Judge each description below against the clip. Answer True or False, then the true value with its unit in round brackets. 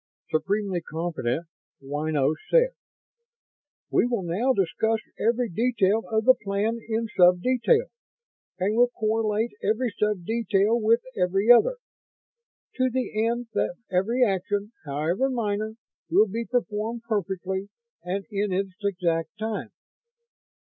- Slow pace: True (120 wpm)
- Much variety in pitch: False (4.0 semitones)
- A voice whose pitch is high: True (210 Hz)